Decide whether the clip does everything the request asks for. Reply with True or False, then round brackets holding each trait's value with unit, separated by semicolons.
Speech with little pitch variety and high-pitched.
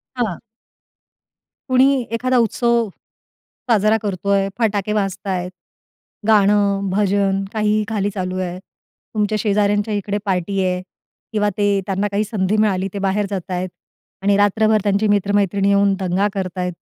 True (1.6 semitones; 200 Hz)